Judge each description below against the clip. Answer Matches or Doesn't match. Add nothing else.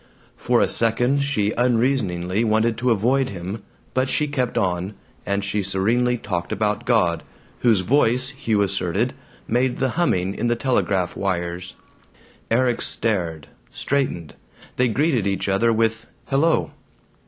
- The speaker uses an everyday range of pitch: Matches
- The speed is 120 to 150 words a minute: Matches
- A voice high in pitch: Doesn't match